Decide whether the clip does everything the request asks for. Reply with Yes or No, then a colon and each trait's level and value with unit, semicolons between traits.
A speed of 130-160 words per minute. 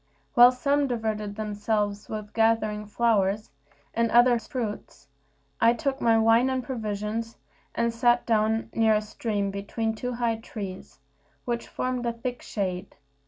Yes: average, 140 wpm